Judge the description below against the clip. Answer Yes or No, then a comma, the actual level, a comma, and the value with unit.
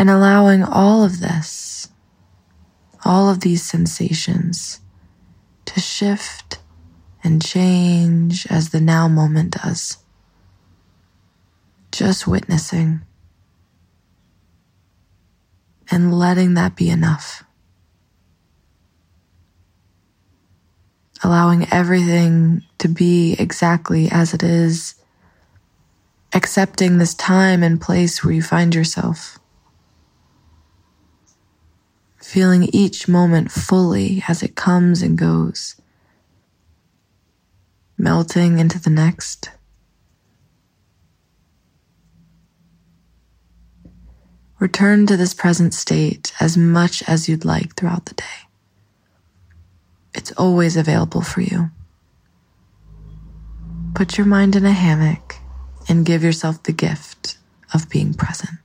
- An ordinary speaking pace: No, slow, 90 wpm